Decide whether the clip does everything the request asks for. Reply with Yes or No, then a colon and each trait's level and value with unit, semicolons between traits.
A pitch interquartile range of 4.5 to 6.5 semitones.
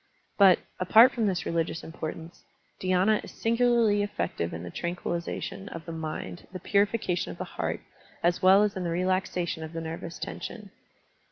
No: average, 3.6 semitones